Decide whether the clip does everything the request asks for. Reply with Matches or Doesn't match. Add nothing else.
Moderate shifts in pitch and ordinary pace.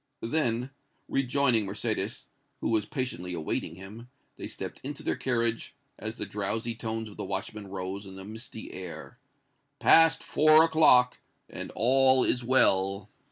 Matches